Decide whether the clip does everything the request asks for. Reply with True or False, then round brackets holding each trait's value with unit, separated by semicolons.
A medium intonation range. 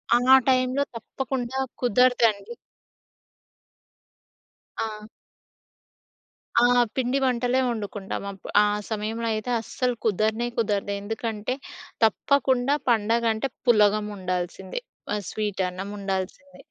True (3.4 semitones)